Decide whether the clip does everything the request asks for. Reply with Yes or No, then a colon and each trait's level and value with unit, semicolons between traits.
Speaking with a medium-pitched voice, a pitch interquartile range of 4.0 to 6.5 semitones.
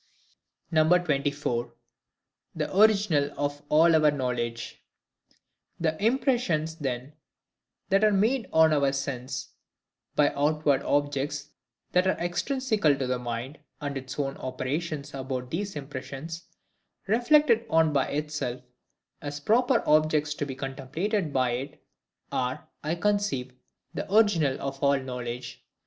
Yes: medium, 145 Hz; average, 4.6 semitones